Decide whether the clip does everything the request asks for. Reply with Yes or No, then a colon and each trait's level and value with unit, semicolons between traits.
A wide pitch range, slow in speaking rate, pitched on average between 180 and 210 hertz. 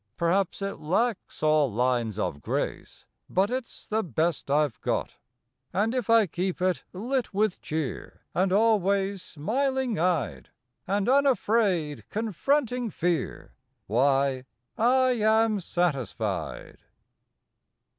Yes: wide, 6.7 semitones; slow, 115 wpm; high, 190 Hz